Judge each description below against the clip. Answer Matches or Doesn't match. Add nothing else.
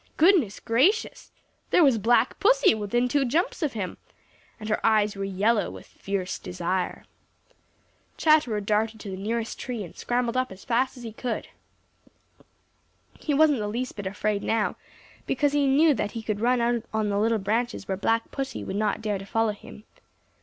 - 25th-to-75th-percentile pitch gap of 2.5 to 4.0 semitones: Matches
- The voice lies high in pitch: Matches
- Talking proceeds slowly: Doesn't match